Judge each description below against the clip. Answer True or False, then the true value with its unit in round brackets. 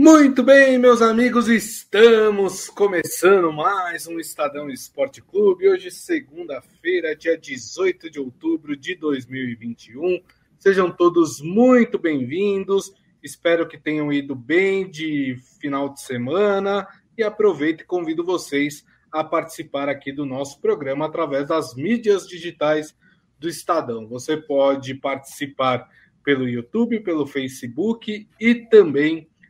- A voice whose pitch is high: False (170 Hz)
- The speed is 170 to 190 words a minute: False (120 wpm)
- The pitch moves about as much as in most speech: False (8.3 semitones)